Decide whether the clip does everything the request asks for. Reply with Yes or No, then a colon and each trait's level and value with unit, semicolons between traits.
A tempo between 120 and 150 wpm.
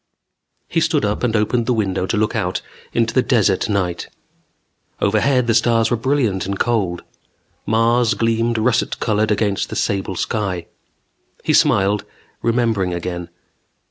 Yes: average, 140 wpm